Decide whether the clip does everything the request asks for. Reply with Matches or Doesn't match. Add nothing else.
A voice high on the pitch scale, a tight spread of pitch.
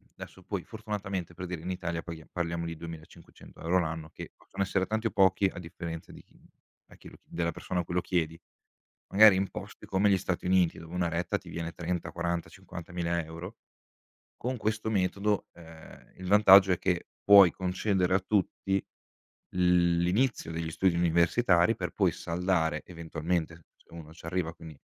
Doesn't match